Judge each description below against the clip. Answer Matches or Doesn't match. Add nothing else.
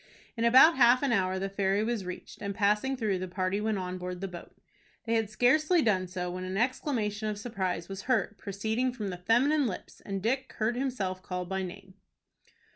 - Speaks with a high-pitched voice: Matches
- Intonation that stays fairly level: Doesn't match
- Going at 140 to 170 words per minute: Doesn't match